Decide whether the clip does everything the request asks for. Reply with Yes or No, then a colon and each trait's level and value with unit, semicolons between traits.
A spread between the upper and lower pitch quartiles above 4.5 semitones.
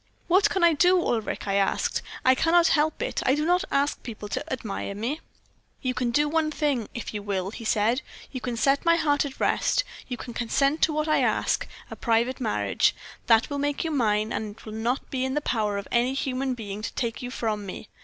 Yes: average, 5.1 semitones